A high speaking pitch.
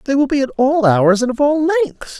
Yes: very high, 270 Hz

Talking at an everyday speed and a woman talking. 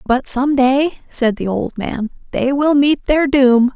Yes: average, 175 wpm; female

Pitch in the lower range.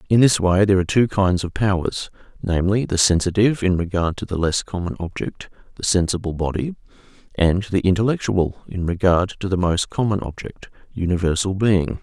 Yes: very low, 95 Hz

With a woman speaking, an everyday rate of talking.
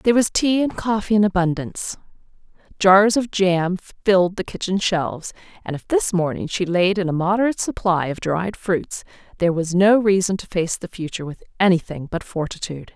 Yes: female; average, 180 wpm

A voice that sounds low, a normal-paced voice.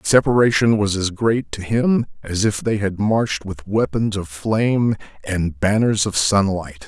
Yes: low, 100 Hz; average, 175 wpm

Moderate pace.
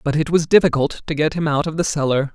No: fast, 280 wpm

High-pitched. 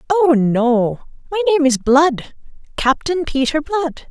Yes: very high, 290 Hz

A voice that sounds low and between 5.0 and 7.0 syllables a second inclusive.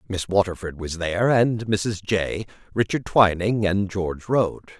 No: low, 100 Hz; 4.3 syllables/s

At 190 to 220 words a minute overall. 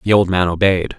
No: fast, 245 wpm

